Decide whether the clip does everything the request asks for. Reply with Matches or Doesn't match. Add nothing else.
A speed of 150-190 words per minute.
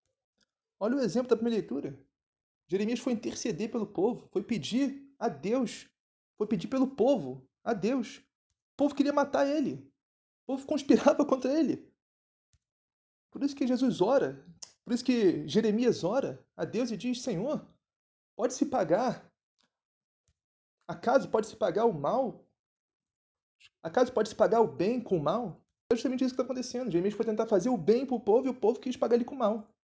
Matches